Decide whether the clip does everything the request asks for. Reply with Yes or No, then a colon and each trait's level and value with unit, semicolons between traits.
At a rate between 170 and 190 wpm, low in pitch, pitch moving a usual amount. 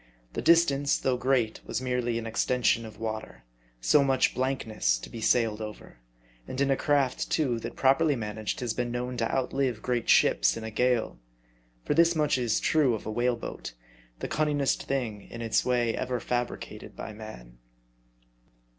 Yes: average, 180 wpm; low, 125 Hz; average, 3.3 semitones